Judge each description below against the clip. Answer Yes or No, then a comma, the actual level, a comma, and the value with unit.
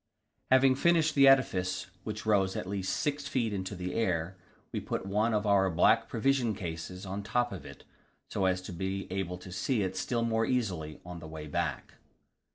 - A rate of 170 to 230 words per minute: Yes, average, 195 wpm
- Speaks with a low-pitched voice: Yes, low, 100 Hz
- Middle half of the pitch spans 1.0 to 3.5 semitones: No, average, 4.3 semitones